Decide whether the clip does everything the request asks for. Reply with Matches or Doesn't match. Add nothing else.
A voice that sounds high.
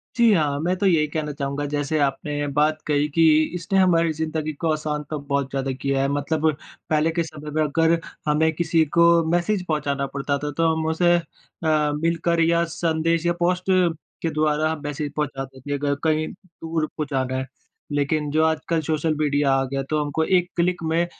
Doesn't match